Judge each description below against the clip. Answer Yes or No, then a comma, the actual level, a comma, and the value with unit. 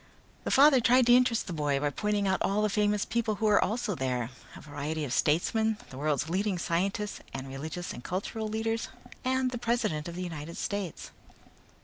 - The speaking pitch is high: Yes, high, 200 Hz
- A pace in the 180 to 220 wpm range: Yes, average, 190 wpm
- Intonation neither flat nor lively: No, wide, 6.3 semitones